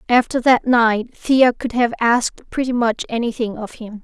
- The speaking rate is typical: Yes, average, 180 wpm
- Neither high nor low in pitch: No, high, 235 Hz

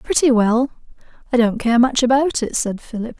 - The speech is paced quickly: No, average, 190 wpm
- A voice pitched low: No, high, 245 Hz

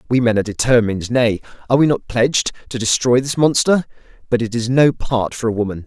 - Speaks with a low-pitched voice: Yes, low, 120 Hz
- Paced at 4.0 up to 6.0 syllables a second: No, 6.3 syllables/s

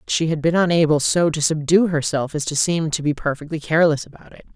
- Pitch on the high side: No, medium, 155 Hz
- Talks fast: Yes, fast, 225 wpm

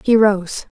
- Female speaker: Yes, female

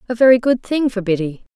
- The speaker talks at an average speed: No, fast, 230 wpm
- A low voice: No, high, 225 Hz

